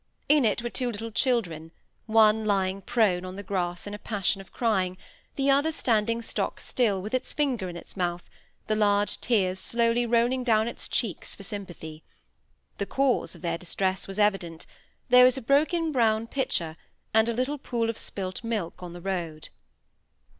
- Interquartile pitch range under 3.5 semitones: No, average, 4.2 semitones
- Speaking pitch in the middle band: No, high, 215 Hz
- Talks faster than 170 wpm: Yes, average, 180 wpm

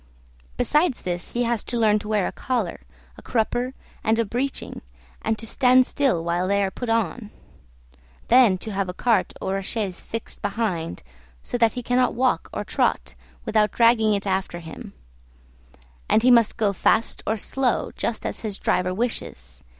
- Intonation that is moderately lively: Yes, average, 4.0 semitones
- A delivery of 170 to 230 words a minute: Yes, average, 175 wpm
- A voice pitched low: No, high, 220 Hz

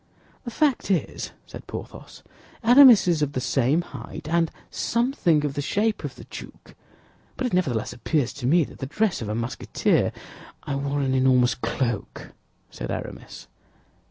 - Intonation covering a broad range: Yes, wide, 6.9 semitones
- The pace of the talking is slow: No, average, 160 wpm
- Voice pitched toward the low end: No, medium, 150 Hz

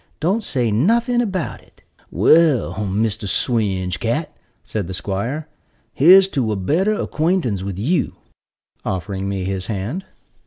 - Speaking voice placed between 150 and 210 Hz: No, low, 115 Hz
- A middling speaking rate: No, slow, 130 wpm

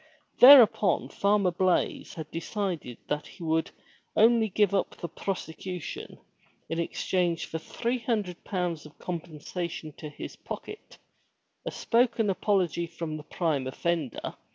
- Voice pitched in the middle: Yes, medium, 175 Hz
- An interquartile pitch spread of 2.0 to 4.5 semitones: Yes, average, 4.0 semitones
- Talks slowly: Yes, slow, 125 wpm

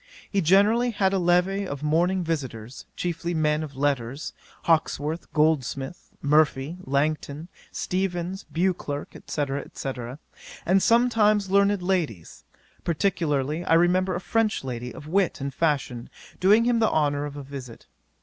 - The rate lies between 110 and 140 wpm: Yes, slow, 135 wpm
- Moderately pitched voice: Yes, medium, 165 Hz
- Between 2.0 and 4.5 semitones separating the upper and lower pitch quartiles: No, average, 5.0 semitones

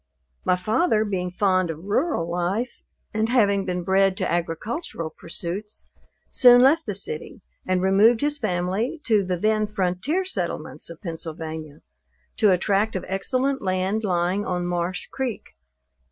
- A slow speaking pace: No, average, 145 wpm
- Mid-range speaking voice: No, high, 195 Hz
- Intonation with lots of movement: No, average, 3.7 semitones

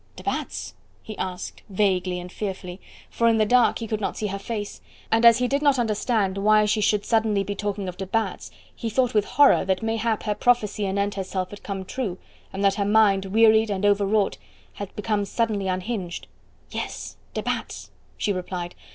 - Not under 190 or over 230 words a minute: Yes, average, 195 wpm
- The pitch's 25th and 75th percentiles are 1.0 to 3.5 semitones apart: Yes, narrow, 2.5 semitones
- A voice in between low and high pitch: No, high, 205 Hz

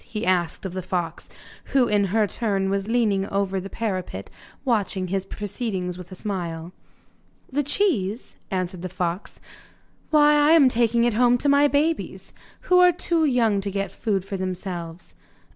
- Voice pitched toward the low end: No, high, 200 Hz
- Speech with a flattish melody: No, average, 4.8 semitones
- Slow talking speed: No, average, 165 wpm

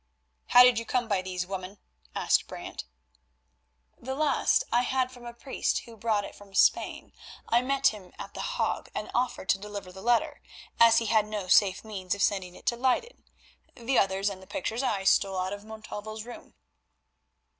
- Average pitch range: Yes, average, 3.9 semitones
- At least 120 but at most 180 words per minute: No, average, 190 wpm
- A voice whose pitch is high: Yes, high, 215 Hz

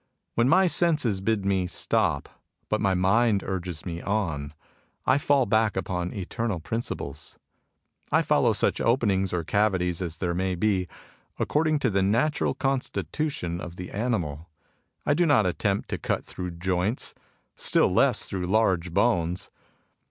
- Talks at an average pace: Yes, average, 150 wpm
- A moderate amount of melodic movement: Yes, average, 4.5 semitones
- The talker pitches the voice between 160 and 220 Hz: No, very low, 95 Hz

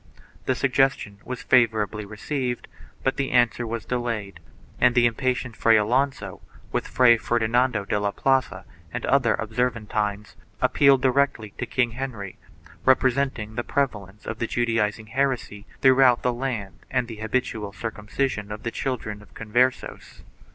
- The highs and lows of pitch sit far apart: No, average, 3.2 semitones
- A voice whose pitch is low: Yes, low, 120 Hz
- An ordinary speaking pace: Yes, average, 145 wpm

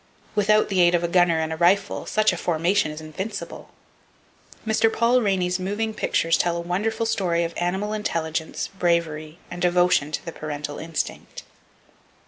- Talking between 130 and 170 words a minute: Yes, average, 160 wpm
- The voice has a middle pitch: Yes, medium, 175 Hz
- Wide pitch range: No, average, 3.5 semitones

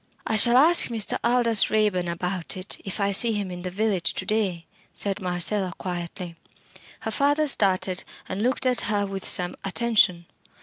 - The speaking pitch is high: Yes, high, 200 Hz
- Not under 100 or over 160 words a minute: No, average, 170 wpm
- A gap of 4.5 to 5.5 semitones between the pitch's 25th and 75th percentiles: No, average, 3.8 semitones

